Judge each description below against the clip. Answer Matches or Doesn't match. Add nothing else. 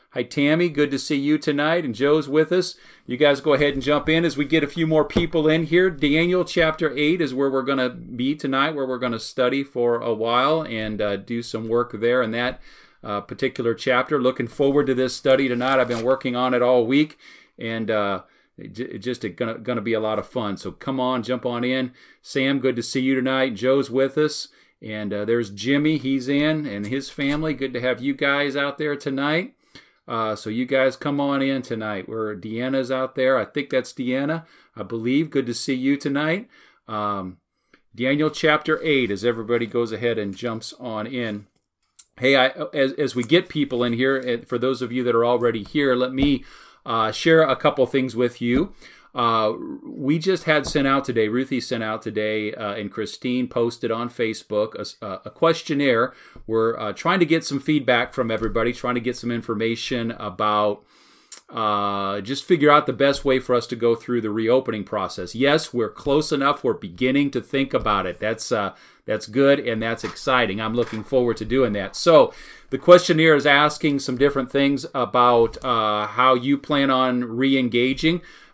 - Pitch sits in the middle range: Doesn't match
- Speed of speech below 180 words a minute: Doesn't match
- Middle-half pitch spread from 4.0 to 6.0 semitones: Doesn't match